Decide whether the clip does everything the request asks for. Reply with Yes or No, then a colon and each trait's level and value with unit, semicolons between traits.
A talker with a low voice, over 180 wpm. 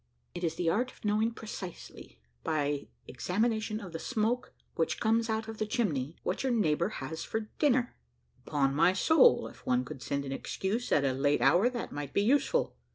No: high, 195 Hz; average, 190 wpm